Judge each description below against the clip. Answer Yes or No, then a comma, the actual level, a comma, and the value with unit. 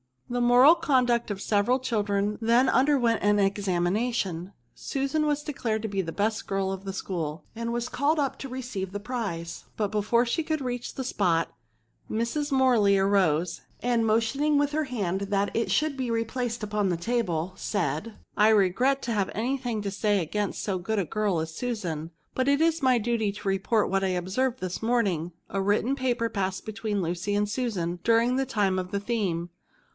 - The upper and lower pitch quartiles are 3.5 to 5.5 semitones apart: Yes, average, 4.2 semitones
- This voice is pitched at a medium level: No, high, 215 Hz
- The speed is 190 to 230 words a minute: Yes, average, 195 wpm